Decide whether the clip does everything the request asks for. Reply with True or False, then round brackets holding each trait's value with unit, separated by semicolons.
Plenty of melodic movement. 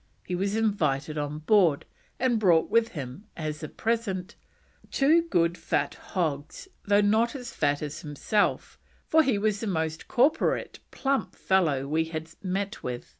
True (6.3 semitones)